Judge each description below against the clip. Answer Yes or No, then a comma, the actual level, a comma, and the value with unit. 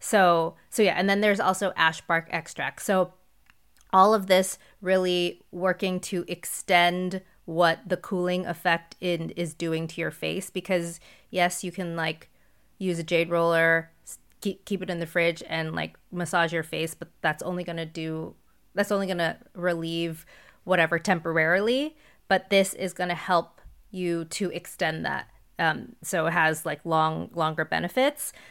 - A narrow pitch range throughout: Yes, narrow, 2.1 semitones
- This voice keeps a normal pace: Yes, average, 160 wpm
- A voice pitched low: No, medium, 175 Hz